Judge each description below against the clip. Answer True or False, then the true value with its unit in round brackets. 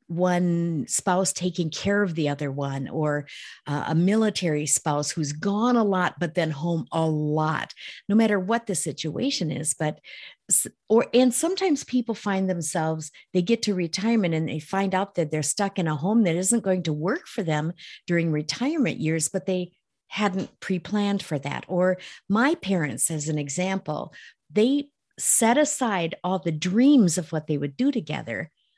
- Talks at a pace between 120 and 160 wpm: False (175 wpm)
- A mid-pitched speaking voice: True (180 Hz)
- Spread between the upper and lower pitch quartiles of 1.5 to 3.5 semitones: False (4.8 semitones)